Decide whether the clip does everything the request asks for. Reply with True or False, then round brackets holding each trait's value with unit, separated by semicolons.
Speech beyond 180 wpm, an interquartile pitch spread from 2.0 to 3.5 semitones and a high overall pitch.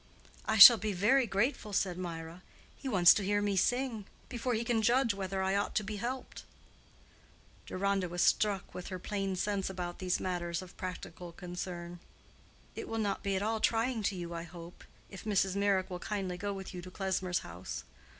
True (190 wpm; 2.9 semitones; 195 Hz)